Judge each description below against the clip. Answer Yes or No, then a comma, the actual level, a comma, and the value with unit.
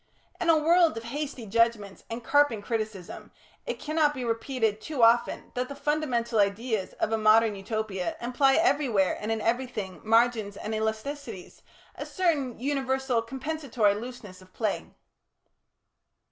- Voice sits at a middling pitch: No, high, 230 Hz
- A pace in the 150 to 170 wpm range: No, average, 140 wpm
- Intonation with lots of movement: No, average, 4.0 semitones